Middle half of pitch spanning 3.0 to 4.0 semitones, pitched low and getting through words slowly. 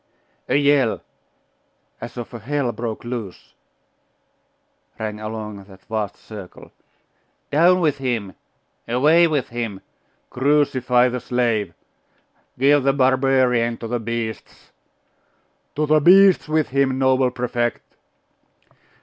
Yes: average, 3.7 semitones; low, 125 Hz; slow, 110 wpm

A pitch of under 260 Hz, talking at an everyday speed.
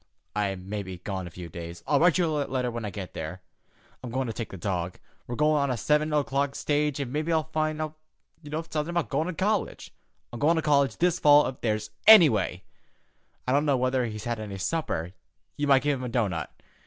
No: low, 135 Hz; fast, 225 wpm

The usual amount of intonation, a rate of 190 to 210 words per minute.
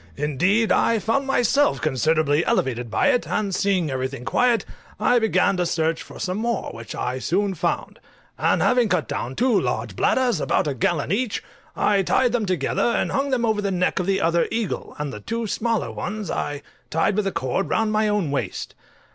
No: wide, 6.7 semitones; average, 195 wpm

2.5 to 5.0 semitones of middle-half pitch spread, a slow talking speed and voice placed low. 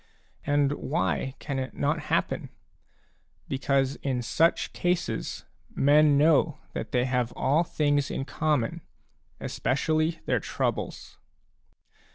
No: average, 2.8 semitones; slow, 110 wpm; medium, 145 Hz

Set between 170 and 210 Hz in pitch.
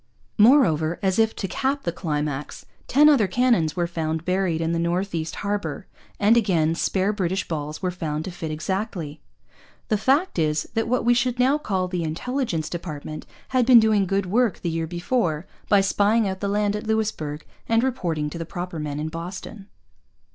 Yes: medium, 185 Hz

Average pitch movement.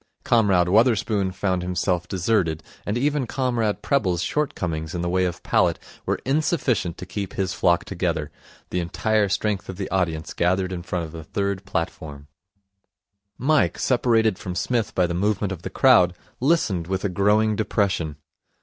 Yes: average, 3.8 semitones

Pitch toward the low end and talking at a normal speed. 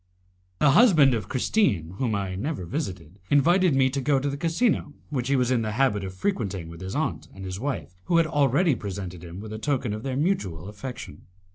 No: low, 125 Hz; fast, 215 wpm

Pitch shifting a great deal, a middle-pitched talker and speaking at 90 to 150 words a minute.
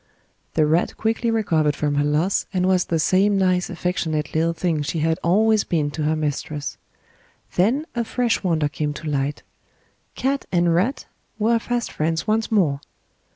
No: wide, 5.7 semitones; medium, 170 Hz; average, 165 wpm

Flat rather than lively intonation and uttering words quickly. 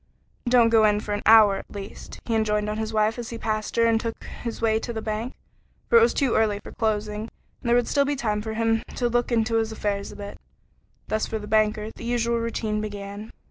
Yes: narrow, 1.6 semitones; fast, 240 wpm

